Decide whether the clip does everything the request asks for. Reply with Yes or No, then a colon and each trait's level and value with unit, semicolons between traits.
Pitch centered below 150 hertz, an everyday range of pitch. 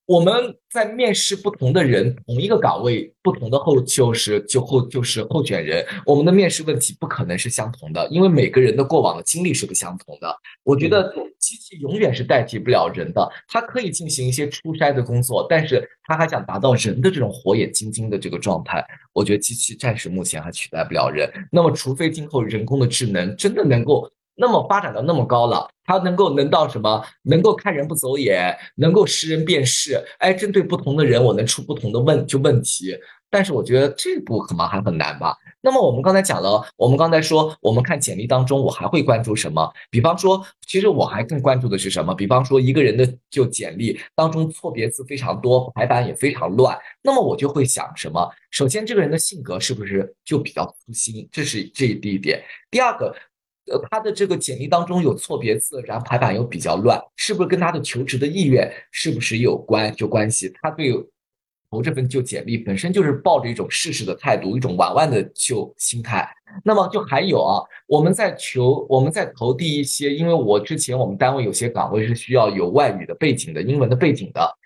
No: medium, 140 Hz; wide, 6.3 semitones